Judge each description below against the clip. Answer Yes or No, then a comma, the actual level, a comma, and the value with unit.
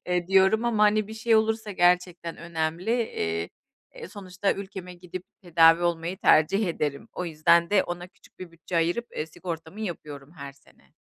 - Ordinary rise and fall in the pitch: Yes, average, 3.4 semitones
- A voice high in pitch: No, medium, 175 Hz